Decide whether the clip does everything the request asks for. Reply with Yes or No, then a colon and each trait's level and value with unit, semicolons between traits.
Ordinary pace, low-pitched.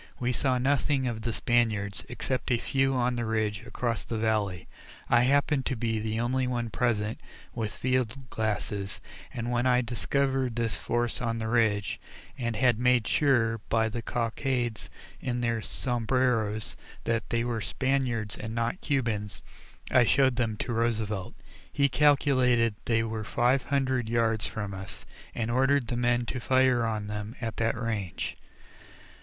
Yes: average, 160 wpm; low, 120 Hz